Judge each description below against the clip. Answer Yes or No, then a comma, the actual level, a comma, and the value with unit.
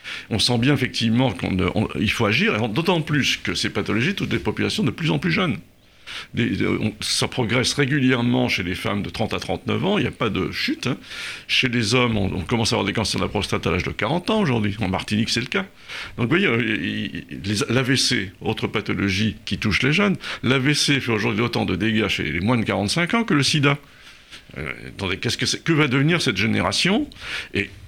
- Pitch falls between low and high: No, low, 110 Hz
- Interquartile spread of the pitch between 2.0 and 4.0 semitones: No, average, 4.5 semitones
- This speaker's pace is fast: Yes, fast, 225 wpm